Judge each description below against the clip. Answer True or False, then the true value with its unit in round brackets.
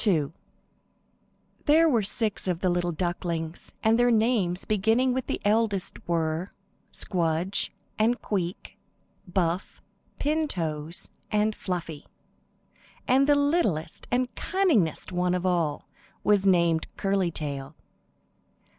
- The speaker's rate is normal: False (115 wpm)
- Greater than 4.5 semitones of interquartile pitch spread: True (5.1 semitones)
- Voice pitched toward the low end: False (185 Hz)